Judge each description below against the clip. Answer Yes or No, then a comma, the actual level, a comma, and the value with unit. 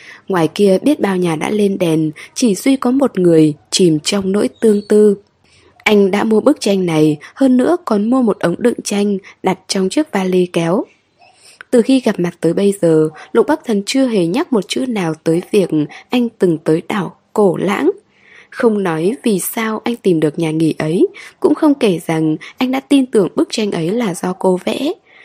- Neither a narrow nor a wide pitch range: No, wide, 5.9 semitones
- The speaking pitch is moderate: No, high, 200 Hz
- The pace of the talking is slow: No, average, 205 wpm